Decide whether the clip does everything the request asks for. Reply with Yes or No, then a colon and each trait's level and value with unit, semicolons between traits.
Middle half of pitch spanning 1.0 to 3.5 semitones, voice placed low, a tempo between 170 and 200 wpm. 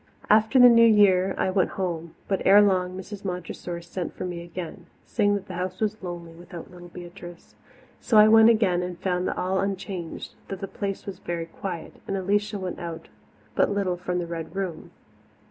No: narrow, 2.4 semitones; medium, 185 Hz; average, 190 wpm